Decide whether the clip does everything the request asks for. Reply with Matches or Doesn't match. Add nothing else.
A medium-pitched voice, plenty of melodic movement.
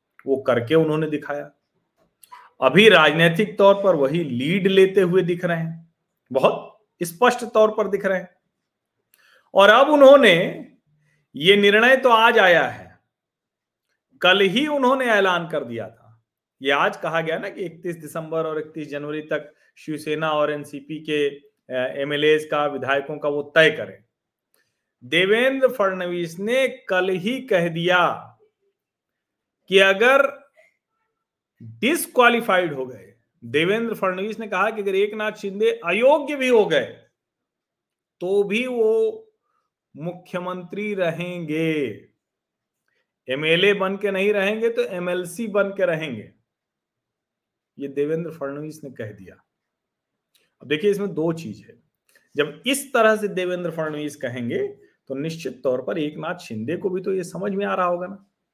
Matches